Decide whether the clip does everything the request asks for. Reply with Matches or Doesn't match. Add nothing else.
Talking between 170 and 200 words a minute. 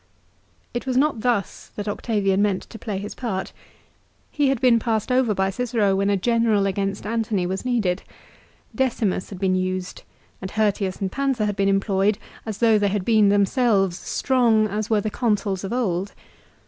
Matches